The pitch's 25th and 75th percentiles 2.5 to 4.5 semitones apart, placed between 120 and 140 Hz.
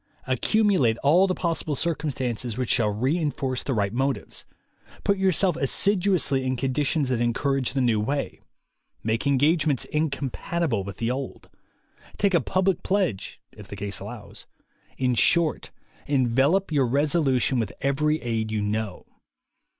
No: average, 5.1 semitones; low, 135 Hz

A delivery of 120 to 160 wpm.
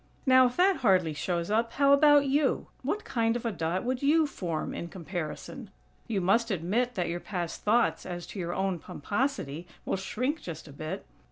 No: average, 190 wpm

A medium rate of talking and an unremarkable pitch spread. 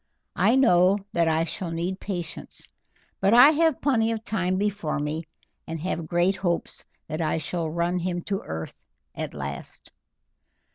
Yes: average, 155 wpm; average, 3.6 semitones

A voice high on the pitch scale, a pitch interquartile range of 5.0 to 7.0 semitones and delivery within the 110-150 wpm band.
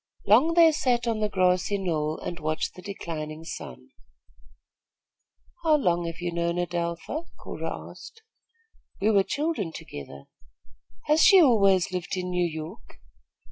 No: medium, 180 Hz; wide, 5.5 semitones; average, 140 wpm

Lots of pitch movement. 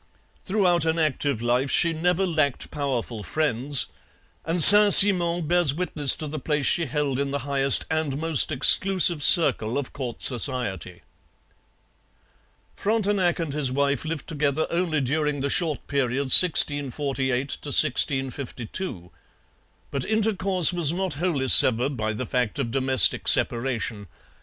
No: average, 4.3 semitones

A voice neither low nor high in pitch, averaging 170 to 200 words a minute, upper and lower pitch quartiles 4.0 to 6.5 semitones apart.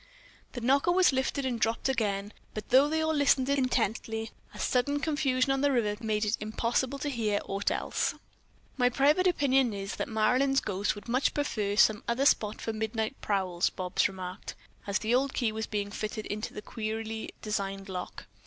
No: high, 225 Hz; average, 180 wpm; average, 4.3 semitones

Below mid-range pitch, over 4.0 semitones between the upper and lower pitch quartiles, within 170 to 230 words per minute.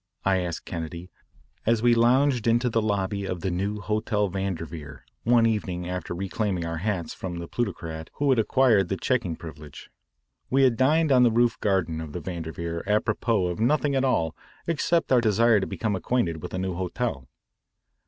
Yes: low, 100 Hz; average, 5.3 semitones; average, 180 wpm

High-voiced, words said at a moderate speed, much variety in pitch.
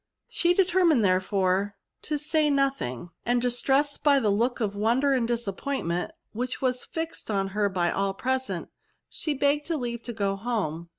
Yes: high, 240 Hz; average, 165 wpm; wide, 6.1 semitones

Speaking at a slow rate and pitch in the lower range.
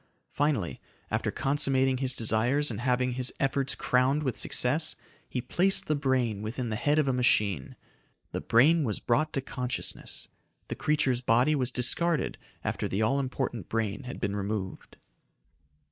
No: average, 155 wpm; low, 130 Hz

